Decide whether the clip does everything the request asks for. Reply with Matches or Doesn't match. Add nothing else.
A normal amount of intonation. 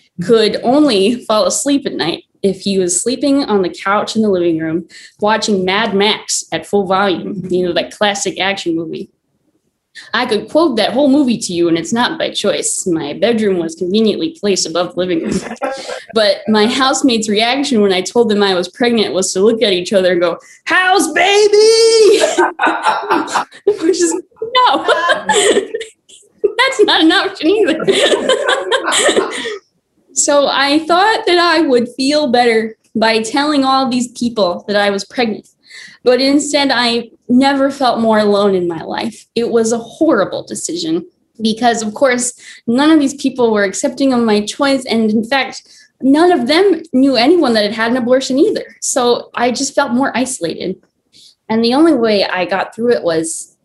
Doesn't match